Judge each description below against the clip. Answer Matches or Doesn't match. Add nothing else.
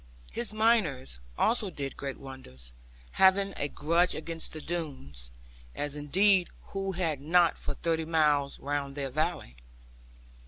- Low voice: Doesn't match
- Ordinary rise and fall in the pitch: Matches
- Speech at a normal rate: Doesn't match